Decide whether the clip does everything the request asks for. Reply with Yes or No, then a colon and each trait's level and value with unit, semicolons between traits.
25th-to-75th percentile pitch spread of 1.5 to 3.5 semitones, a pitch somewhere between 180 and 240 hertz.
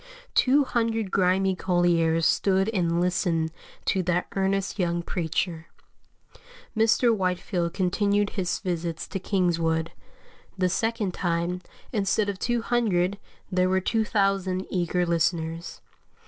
Yes: narrow, 2.6 semitones; medium, 185 Hz